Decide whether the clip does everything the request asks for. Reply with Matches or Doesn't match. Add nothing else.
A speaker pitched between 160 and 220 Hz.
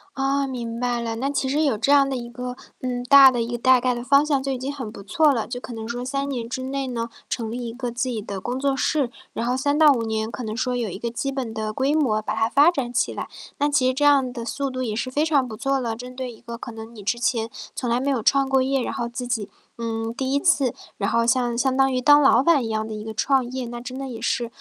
Doesn't match